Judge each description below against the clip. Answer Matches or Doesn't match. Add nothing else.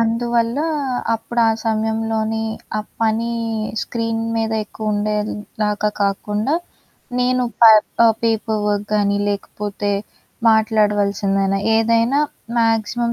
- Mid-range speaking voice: Doesn't match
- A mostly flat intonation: Matches